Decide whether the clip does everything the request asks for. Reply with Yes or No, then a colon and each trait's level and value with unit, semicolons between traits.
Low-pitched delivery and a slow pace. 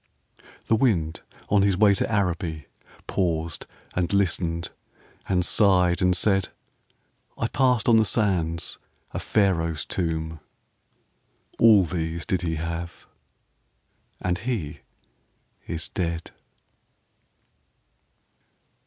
Yes: very low, 90 Hz; slow, 100 wpm